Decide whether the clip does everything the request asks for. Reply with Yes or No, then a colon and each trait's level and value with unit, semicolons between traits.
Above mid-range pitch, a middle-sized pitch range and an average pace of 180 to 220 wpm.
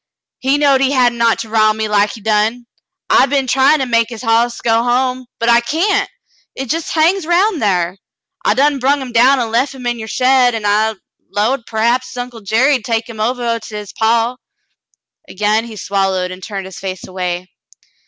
Yes: high, 235 Hz; average, 3.3 semitones; average, 195 wpm